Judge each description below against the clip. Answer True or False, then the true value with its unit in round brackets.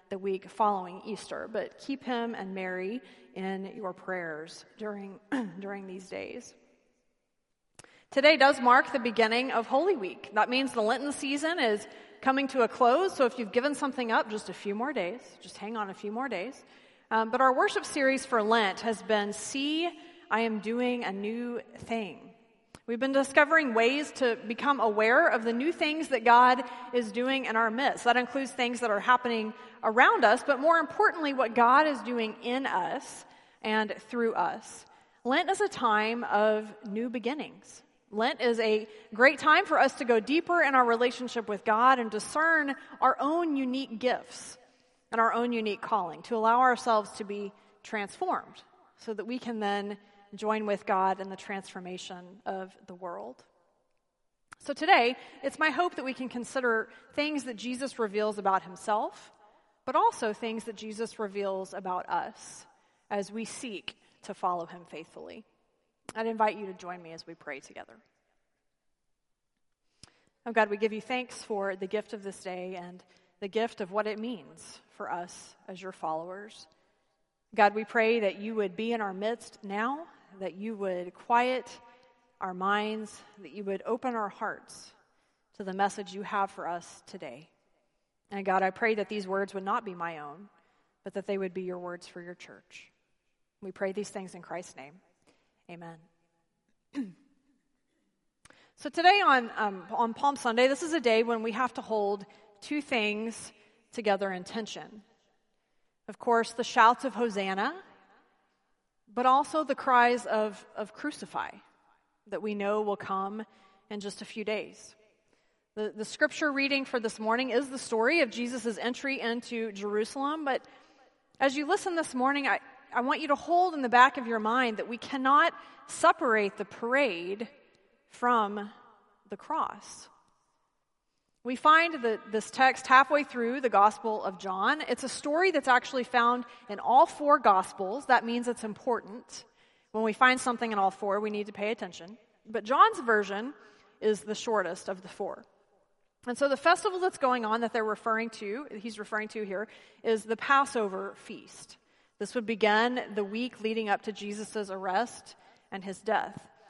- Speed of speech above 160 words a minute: True (170 wpm)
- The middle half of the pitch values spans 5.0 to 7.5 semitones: False (3.9 semitones)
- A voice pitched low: False (225 Hz)